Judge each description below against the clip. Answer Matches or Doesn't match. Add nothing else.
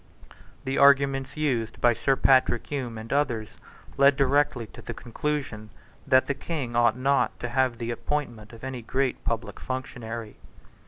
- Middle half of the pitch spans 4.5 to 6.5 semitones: Doesn't match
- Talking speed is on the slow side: Doesn't match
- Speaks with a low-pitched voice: Matches